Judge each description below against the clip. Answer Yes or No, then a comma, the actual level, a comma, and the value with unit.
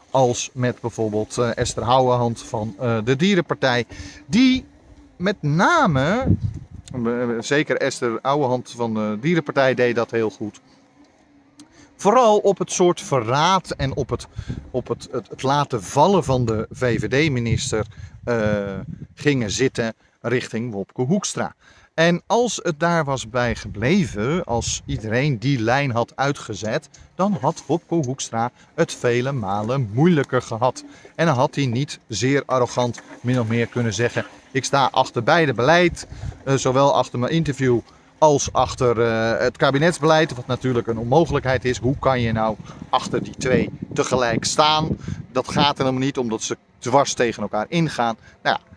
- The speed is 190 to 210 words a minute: No, average, 145 wpm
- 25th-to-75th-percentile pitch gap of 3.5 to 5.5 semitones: Yes, average, 4.4 semitones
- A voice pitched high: No, low, 130 Hz